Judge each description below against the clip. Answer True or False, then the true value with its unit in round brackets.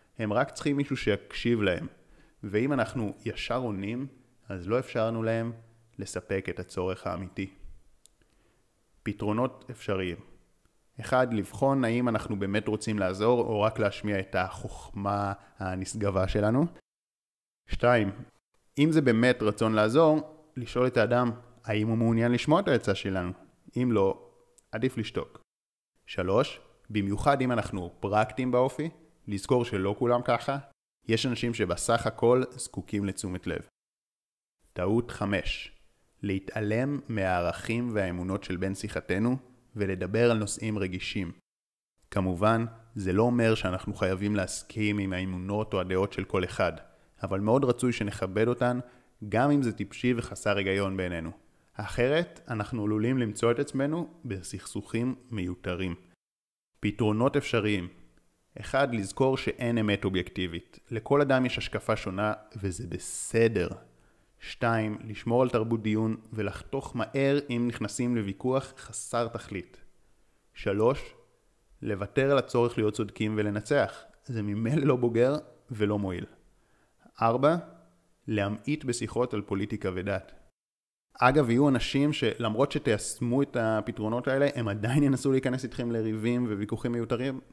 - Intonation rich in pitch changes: False (3.7 semitones)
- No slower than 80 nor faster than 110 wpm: False (120 wpm)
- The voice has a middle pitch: False (110 Hz)